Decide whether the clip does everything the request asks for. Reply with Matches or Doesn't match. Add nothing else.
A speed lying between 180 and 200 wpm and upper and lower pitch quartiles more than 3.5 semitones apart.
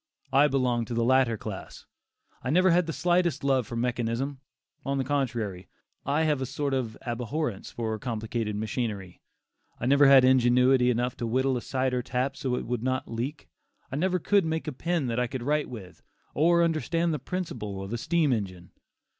Matches